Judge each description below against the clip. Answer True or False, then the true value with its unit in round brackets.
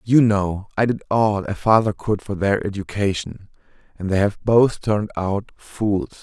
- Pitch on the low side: True (100 Hz)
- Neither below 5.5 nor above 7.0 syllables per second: False (4.4 syllables/s)